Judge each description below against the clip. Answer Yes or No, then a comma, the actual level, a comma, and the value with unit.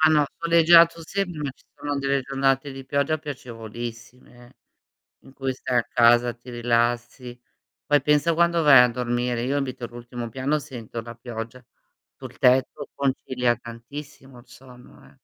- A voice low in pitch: Yes, low, 130 Hz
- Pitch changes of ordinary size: Yes, average, 3.1 semitones